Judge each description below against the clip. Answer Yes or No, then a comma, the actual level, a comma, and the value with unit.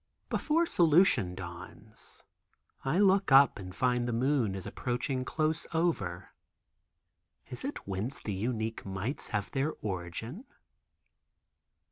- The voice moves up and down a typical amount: No, wide, 7.8 semitones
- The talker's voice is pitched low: Yes, low, 120 Hz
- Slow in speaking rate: Yes, slow, 115 wpm